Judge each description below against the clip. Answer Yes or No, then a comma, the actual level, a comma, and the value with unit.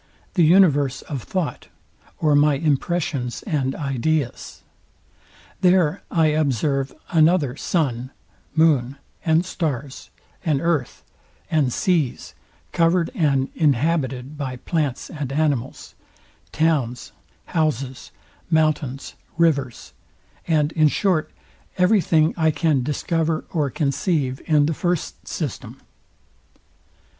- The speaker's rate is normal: No, slow, 100 wpm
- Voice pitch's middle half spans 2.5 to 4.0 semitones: Yes, average, 3.2 semitones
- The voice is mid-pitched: Yes, medium, 150 Hz